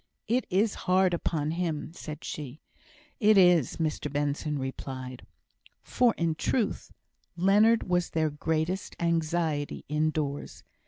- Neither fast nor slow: No, slow, 115 wpm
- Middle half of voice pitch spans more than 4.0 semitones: No, average, 3.6 semitones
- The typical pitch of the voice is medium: Yes, medium, 160 Hz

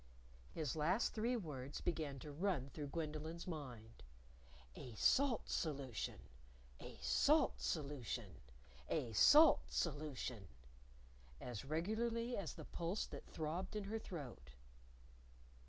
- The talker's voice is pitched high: No, medium, 155 Hz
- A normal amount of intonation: No, wide, 6.6 semitones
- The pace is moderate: No, slow, 110 wpm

